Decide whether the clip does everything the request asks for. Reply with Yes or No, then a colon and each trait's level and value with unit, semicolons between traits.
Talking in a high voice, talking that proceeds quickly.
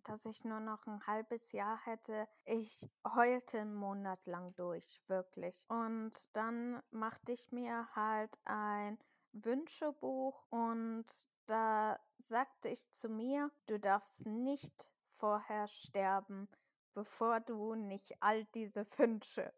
No: high, 220 Hz; slow, 125 wpm